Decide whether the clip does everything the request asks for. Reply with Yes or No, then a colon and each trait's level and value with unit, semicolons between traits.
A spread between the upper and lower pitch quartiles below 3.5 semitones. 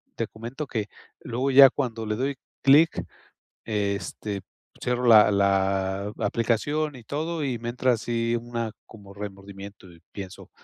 No: average, 4.1 semitones